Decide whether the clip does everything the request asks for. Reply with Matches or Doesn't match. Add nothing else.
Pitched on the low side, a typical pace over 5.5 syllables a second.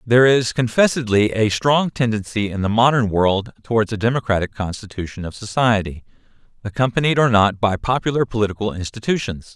Matches